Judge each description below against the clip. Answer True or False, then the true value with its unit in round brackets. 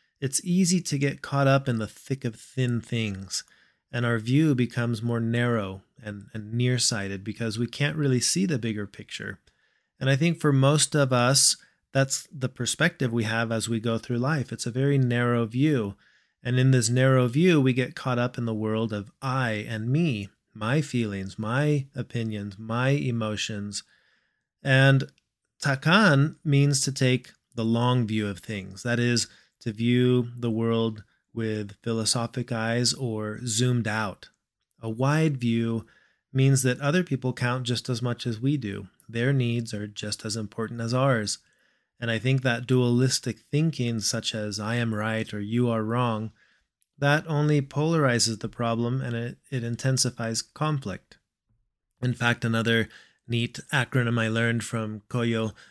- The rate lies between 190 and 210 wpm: False (165 wpm)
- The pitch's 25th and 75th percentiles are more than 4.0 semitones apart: False (3.0 semitones)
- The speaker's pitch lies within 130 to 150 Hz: False (120 Hz)